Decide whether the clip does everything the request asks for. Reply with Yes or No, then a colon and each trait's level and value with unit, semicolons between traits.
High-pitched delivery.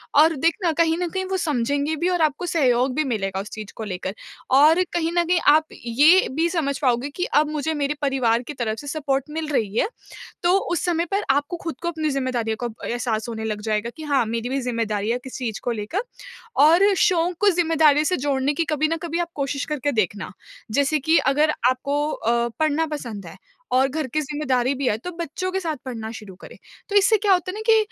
Yes: very high, 285 Hz